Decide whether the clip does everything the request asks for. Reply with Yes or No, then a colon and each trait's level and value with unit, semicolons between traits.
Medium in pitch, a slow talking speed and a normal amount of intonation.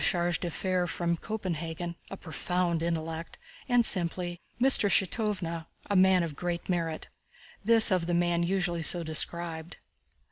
No: medium, 175 Hz; slow, 115 wpm; narrow, 2.0 semitones